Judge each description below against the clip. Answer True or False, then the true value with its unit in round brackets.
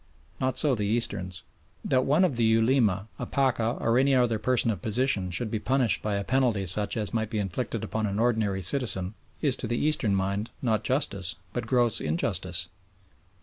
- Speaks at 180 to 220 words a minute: True (190 wpm)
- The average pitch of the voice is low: True (110 Hz)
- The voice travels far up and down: False (4.3 semitones)